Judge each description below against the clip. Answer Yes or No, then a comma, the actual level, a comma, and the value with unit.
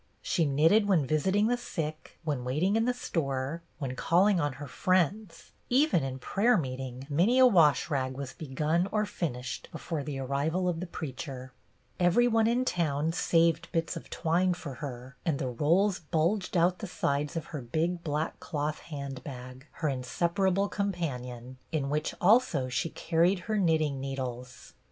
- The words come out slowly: No, average, 165 wpm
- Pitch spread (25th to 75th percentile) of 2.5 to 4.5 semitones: No, average, 5.1 semitones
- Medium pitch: Yes, medium, 160 Hz